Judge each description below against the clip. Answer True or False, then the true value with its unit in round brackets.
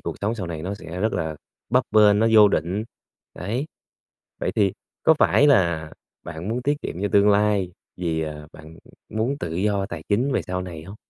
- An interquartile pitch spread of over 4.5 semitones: False (4.2 semitones)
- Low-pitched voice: True (100 Hz)